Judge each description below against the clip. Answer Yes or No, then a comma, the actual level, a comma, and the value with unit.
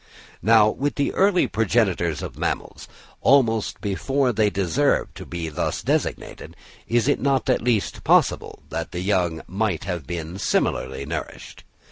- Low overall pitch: Yes, low, 105 Hz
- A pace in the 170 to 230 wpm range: No, average, 145 wpm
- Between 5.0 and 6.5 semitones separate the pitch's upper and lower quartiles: Yes, wide, 5.6 semitones